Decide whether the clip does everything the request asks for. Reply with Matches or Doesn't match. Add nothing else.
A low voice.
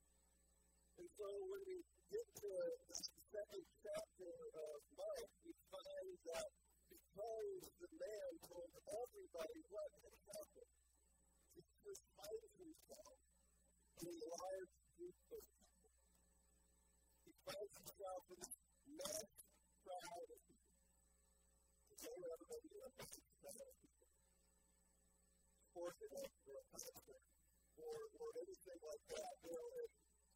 Doesn't match